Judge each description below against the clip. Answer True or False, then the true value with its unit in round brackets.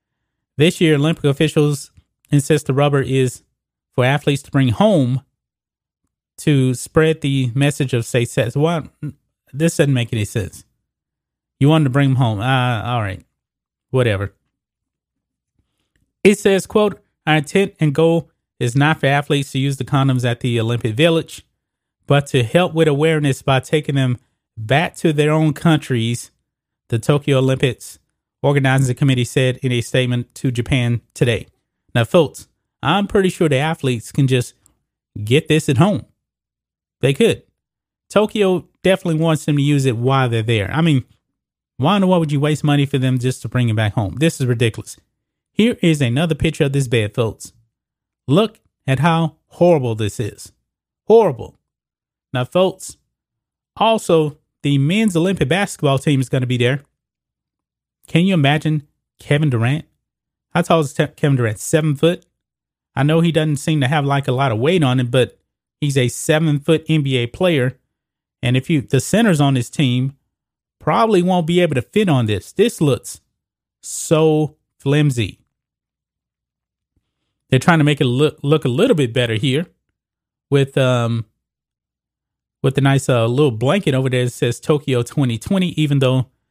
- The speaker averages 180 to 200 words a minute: False (165 wpm)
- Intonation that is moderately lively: True (4.2 semitones)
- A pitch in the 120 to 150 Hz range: True (140 Hz)